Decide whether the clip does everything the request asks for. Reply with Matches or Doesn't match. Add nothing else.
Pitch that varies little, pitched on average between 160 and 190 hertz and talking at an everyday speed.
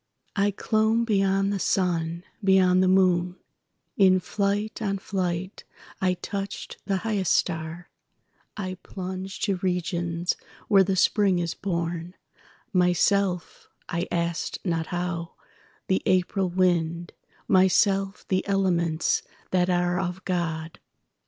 Doesn't match